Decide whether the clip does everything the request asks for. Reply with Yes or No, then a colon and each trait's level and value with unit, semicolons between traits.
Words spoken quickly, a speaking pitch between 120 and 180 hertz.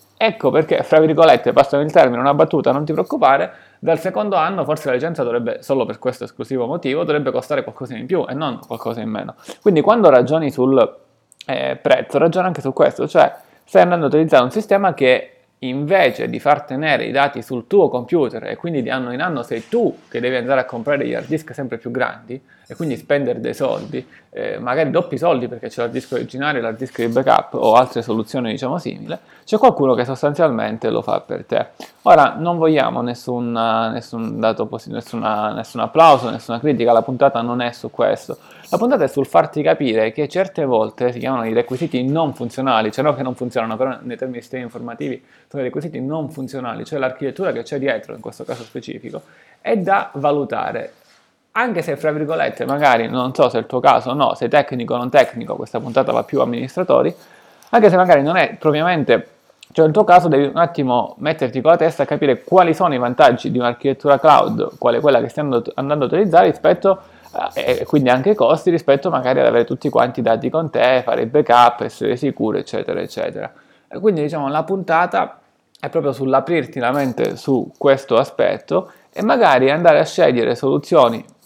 Yes: fast, 200 wpm; low, 135 Hz